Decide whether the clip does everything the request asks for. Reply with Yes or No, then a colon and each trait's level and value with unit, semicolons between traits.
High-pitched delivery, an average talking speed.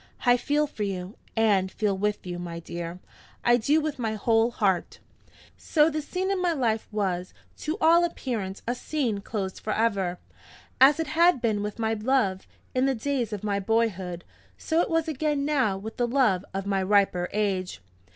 Yes: high, 220 Hz; average, 180 wpm